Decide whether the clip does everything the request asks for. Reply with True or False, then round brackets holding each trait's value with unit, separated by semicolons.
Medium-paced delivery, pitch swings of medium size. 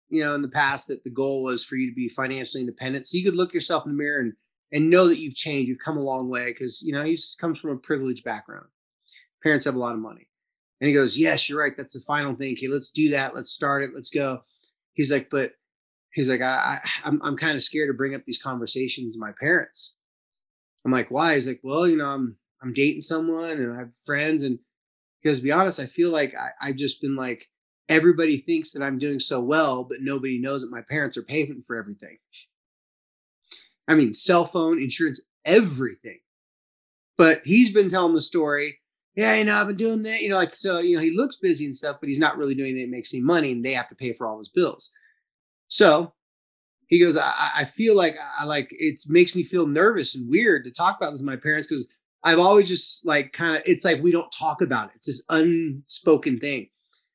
False (235 wpm; 4.1 semitones)